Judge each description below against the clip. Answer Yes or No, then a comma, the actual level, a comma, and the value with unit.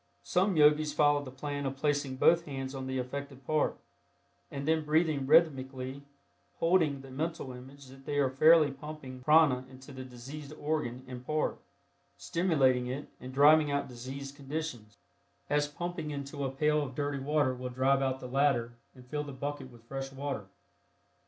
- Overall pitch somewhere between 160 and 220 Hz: No, medium, 140 Hz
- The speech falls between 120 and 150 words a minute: No, average, 170 wpm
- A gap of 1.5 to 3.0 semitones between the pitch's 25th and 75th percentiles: Yes, narrow, 2.4 semitones